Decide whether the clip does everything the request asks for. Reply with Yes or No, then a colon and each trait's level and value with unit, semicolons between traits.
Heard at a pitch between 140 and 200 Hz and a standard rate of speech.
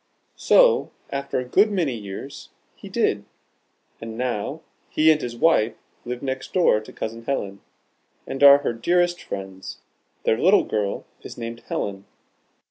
No: low, 125 Hz; average, 145 wpm